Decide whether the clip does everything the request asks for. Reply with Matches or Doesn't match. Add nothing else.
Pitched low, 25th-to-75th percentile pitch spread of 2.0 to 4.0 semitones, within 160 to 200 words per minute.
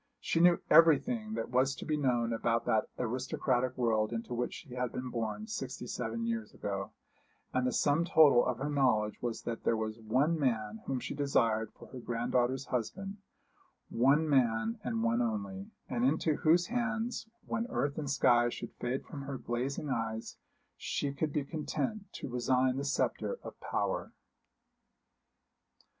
Doesn't match